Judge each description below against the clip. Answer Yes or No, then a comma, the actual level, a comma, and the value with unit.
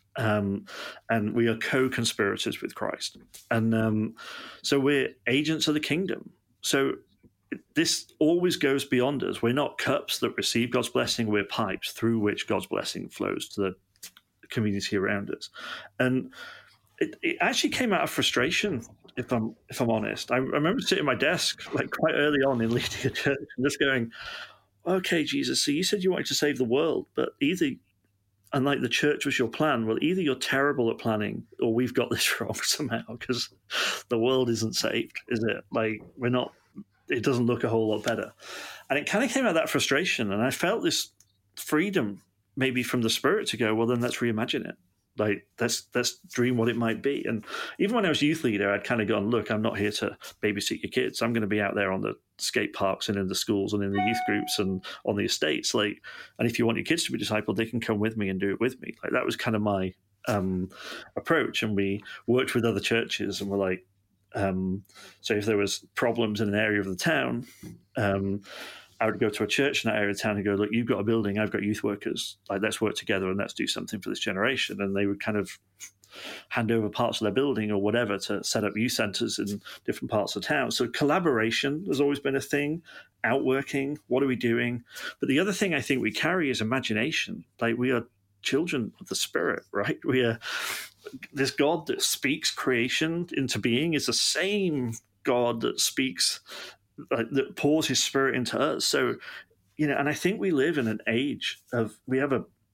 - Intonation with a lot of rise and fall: No, average, 4.3 semitones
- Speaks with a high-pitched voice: No, low, 115 Hz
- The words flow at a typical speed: No, fast, 215 wpm